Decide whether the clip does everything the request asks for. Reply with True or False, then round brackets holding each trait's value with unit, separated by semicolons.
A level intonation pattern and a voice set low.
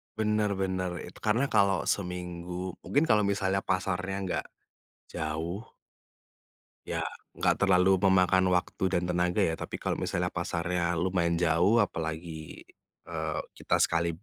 True (1.9 semitones; 90 Hz)